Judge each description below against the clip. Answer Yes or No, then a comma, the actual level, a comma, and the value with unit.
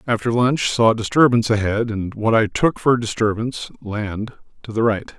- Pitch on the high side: No, low, 115 Hz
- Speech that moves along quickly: No, average, 175 wpm